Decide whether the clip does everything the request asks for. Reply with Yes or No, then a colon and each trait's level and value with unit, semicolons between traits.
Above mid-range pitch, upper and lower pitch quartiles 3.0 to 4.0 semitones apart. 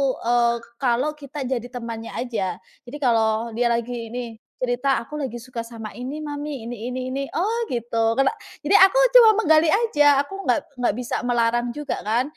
Yes: high, 245 Hz; average, 3.7 semitones